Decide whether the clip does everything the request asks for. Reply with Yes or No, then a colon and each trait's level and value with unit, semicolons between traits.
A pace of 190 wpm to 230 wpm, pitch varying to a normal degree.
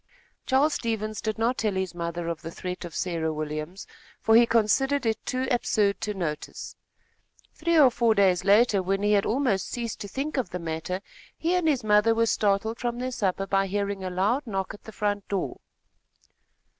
Yes: average, 195 wpm; average, 4.1 semitones